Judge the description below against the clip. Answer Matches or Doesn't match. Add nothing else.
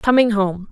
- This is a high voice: Matches